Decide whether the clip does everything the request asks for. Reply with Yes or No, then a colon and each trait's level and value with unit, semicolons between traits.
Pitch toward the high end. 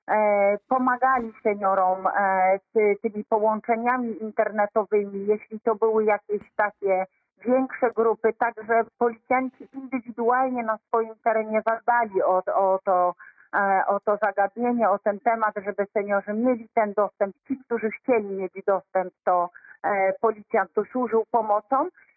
Yes: high, 220 Hz